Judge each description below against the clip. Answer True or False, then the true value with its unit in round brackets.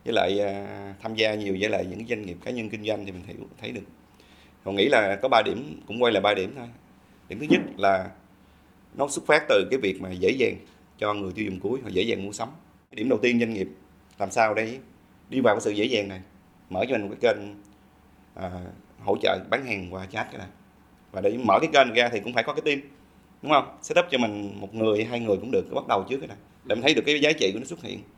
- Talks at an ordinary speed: False (265 wpm)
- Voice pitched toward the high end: False (100 Hz)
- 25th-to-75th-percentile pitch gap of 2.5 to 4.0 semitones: True (3.0 semitones)